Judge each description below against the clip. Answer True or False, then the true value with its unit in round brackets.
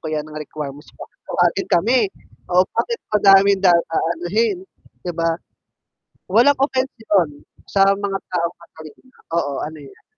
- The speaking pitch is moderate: True (180 Hz)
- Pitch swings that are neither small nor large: True (3.8 semitones)